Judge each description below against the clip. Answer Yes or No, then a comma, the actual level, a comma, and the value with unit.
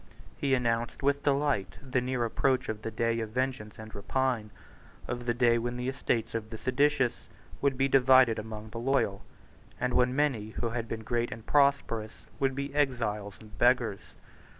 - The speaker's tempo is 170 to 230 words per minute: Yes, average, 175 wpm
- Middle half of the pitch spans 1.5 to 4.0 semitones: Yes, average, 3.1 semitones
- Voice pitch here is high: No, low, 120 Hz